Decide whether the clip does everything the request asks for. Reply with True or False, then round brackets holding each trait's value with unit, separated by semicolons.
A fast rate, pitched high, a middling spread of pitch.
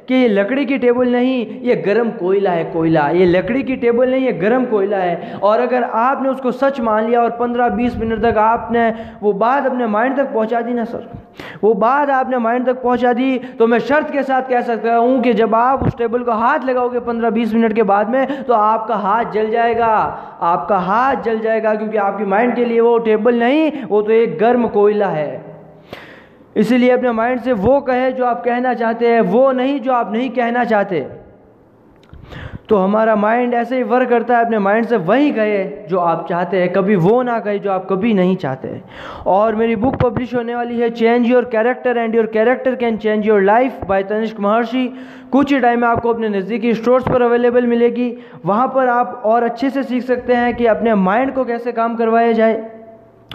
False (210 wpm; 235 Hz; 2.2 semitones)